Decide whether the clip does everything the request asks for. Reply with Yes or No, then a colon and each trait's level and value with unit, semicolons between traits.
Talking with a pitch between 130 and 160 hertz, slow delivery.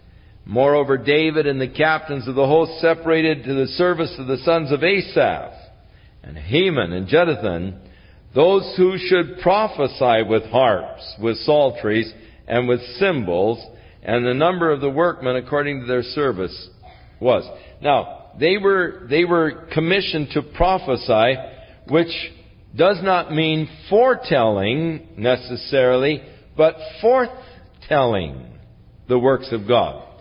Yes: medium, 140 Hz; slow, 125 wpm